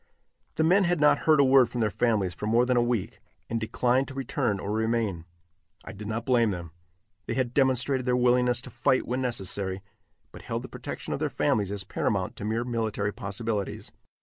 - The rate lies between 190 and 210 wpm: Yes, average, 200 wpm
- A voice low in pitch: Yes, low, 115 Hz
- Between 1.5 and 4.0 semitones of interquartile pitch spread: Yes, average, 3.7 semitones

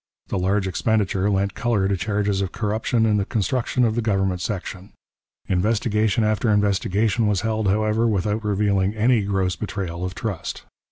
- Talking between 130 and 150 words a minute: No, average, 160 wpm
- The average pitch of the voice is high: No, low, 105 Hz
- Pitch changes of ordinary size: No, narrow, 2.3 semitones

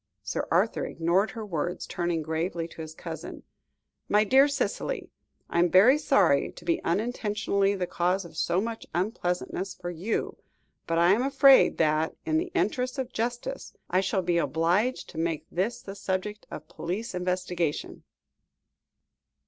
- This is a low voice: No, medium, 185 Hz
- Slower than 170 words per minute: Yes, average, 155 wpm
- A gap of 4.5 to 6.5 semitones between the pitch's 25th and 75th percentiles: Yes, average, 4.9 semitones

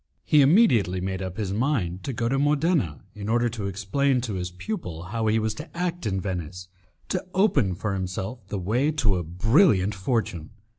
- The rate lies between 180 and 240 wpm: Yes, average, 190 wpm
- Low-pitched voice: Yes, low, 105 Hz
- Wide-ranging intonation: Yes, wide, 6.6 semitones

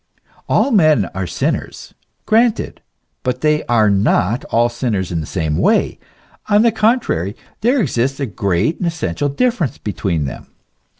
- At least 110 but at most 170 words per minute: Yes, average, 155 wpm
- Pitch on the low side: Yes, low, 125 Hz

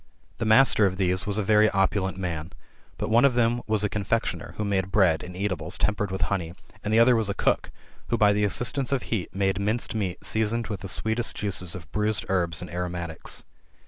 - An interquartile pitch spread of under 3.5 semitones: Yes, average, 3.1 semitones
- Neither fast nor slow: No, fast, 210 wpm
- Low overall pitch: Yes, low, 100 Hz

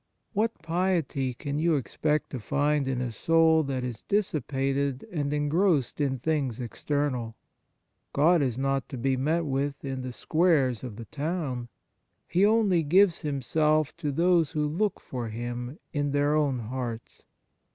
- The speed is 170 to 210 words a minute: No, average, 155 wpm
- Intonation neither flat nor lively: Yes, average, 3.8 semitones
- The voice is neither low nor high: Yes, medium, 145 Hz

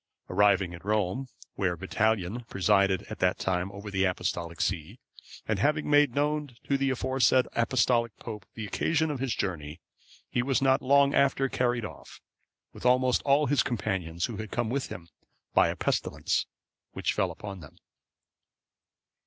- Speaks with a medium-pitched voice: No, low, 115 Hz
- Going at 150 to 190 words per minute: Yes, average, 160 wpm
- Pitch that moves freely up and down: Yes, wide, 5.8 semitones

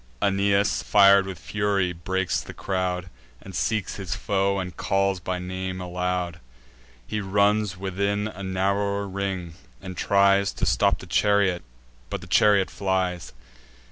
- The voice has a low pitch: Yes, very low, 95 Hz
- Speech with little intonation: Yes, narrow, 1.6 semitones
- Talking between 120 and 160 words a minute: Yes, average, 140 wpm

